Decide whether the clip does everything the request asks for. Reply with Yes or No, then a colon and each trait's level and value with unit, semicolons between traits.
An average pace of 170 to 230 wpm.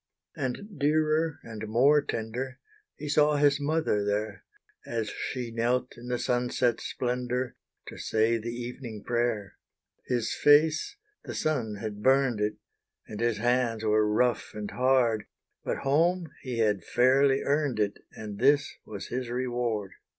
No: average, 145 wpm